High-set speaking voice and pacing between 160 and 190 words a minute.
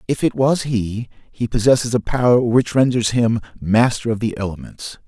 No: low, 115 Hz; average, 175 wpm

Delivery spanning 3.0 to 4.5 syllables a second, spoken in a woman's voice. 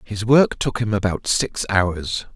No: 3.7 syllables/s; male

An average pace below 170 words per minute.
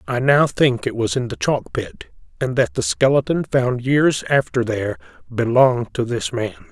No: average, 190 wpm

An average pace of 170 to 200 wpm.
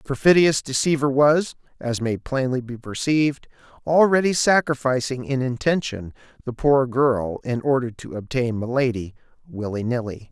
No: slow, 135 wpm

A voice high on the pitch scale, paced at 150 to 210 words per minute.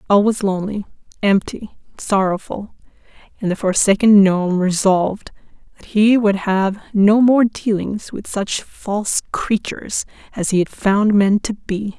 No: high, 200 Hz; average, 140 wpm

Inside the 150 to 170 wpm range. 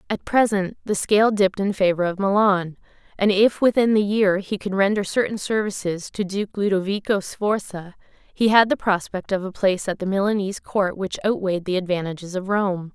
No: average, 185 wpm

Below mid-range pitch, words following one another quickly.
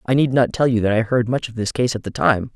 Yes: low, 115 Hz; fast, 355 wpm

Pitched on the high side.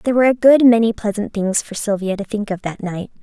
Yes: high, 215 Hz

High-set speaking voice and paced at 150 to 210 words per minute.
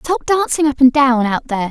No: very high, 270 Hz; fast, 245 wpm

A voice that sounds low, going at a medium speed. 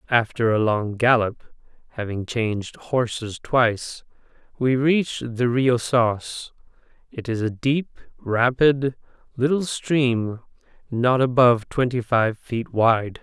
No: low, 120 Hz; slow, 120 wpm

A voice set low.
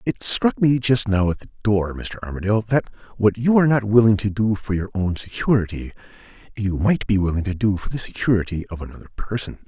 Yes: low, 105 Hz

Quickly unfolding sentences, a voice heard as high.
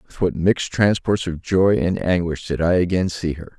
No: fast, 215 wpm; very low, 90 Hz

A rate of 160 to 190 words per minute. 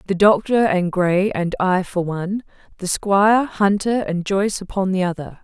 Yes: average, 175 wpm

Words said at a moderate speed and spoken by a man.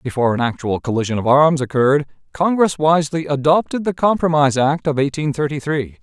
Yes: average, 170 wpm; male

